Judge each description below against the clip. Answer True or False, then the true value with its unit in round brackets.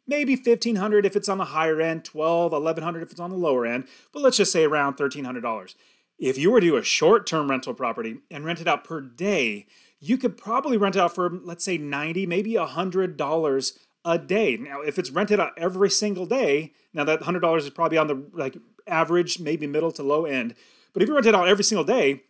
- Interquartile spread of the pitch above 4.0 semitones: True (4.6 semitones)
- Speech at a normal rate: False (220 wpm)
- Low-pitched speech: False (170 Hz)